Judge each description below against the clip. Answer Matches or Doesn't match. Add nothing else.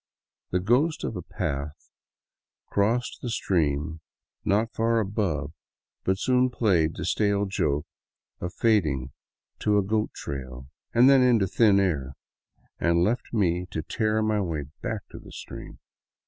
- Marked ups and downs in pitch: Matches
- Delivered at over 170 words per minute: Doesn't match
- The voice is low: Matches